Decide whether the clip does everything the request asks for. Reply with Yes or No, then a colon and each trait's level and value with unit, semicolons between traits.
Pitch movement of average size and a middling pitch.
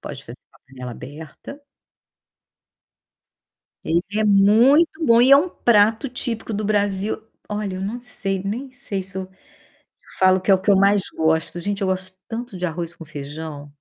No: average, 3.9 semitones; high, 195 Hz